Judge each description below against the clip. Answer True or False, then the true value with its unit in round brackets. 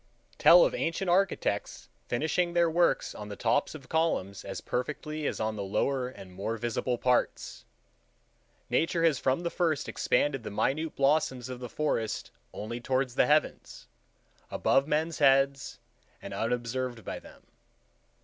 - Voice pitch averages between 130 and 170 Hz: True (135 Hz)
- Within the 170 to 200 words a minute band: False (150 wpm)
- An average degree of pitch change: True (4.9 semitones)